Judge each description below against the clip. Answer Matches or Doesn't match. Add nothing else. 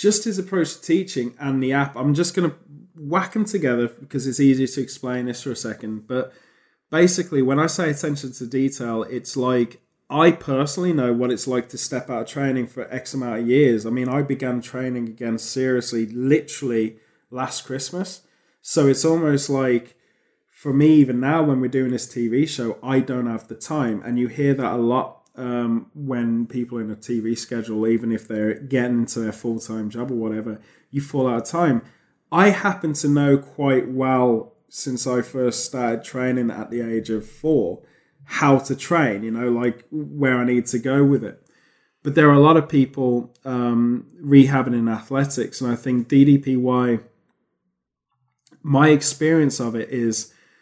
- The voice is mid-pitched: Doesn't match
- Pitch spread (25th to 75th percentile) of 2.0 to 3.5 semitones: Matches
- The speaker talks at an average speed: Matches